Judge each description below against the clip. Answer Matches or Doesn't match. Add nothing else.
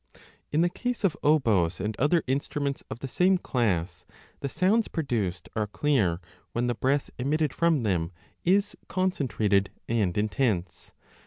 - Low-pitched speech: Matches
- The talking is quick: Doesn't match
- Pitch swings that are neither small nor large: Doesn't match